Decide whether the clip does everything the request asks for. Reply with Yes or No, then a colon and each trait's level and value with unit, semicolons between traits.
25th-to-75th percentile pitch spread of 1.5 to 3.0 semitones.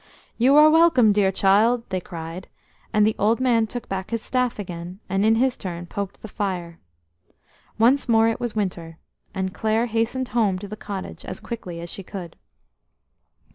No: average, 3.8 semitones